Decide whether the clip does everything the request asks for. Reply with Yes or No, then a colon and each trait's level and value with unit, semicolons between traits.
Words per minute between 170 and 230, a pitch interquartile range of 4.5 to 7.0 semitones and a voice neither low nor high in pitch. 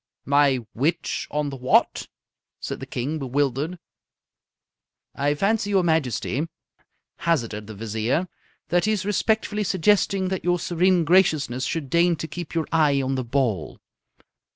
No: average, 140 wpm; average, 5.0 semitones; medium, 155 Hz